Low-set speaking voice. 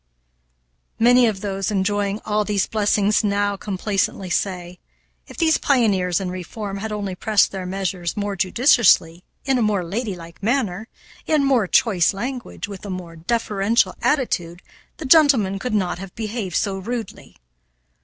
No: high, 205 Hz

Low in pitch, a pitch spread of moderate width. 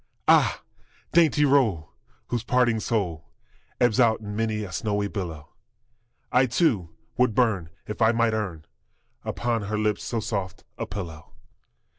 Yes: low, 110 Hz; average, 3.9 semitones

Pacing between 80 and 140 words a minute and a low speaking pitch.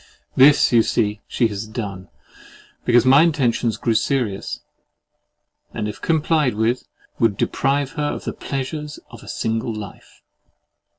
Yes: slow, 135 wpm; low, 120 Hz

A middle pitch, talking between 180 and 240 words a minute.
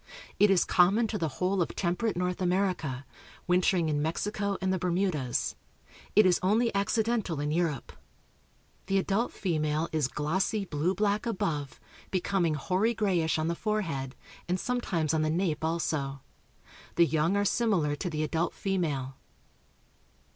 No: medium, 180 Hz; average, 145 wpm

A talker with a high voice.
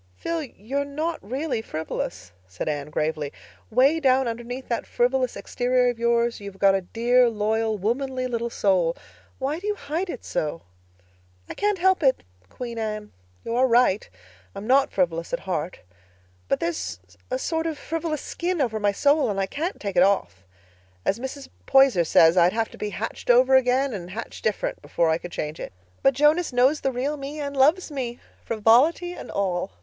Yes: high, 240 Hz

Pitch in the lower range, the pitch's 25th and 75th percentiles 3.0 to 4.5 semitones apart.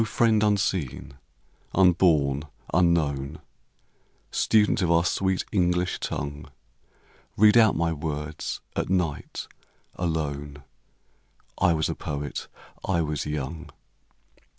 Yes: very low, 85 Hz; average, 4.1 semitones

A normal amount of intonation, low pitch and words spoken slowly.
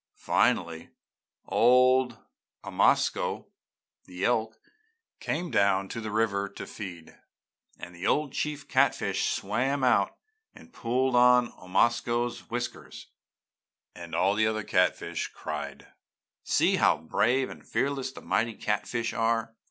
Yes: average, 4.0 semitones; low, 115 Hz; slow, 120 wpm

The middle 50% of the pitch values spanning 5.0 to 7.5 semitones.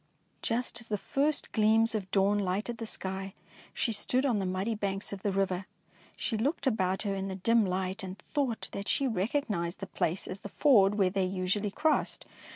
No: average, 3.1 semitones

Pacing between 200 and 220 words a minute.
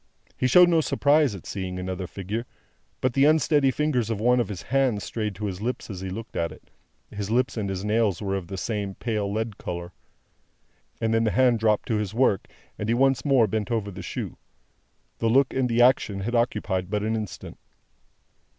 Yes: fast, 205 wpm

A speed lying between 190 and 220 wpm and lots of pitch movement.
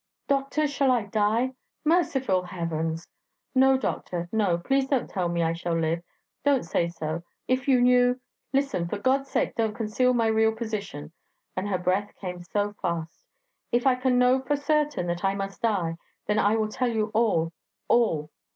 No: average, 175 wpm; wide, 6.6 semitones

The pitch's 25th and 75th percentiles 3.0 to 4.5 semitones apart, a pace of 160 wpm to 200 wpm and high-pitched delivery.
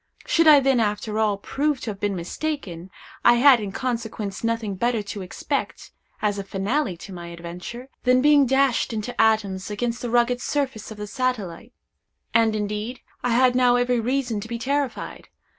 Yes: average, 3.6 semitones; average, 175 wpm; high, 230 Hz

